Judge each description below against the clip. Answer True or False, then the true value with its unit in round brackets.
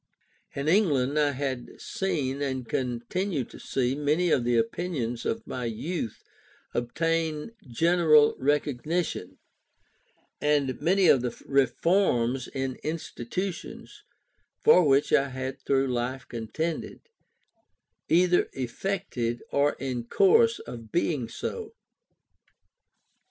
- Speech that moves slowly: True (105 wpm)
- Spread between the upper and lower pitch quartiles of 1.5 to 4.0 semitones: False (5.2 semitones)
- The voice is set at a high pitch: False (140 Hz)